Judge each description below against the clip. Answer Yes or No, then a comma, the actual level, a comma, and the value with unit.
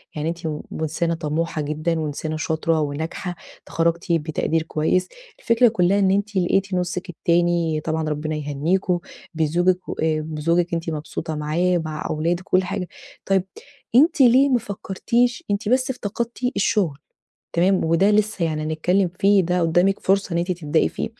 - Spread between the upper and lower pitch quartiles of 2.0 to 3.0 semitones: No, average, 3.6 semitones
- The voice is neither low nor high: Yes, medium, 170 Hz